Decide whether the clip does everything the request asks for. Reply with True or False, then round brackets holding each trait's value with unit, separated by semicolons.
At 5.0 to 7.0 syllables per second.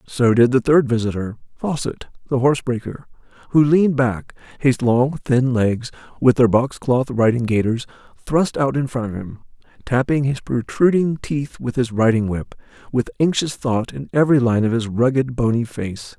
False (4.8 syllables/s)